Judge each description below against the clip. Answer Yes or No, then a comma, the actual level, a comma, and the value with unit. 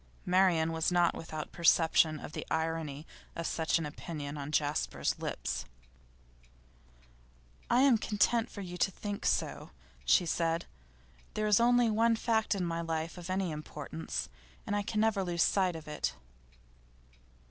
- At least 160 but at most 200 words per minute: No, average, 150 wpm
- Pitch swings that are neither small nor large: Yes, average, 4.3 semitones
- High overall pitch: No, medium, 170 Hz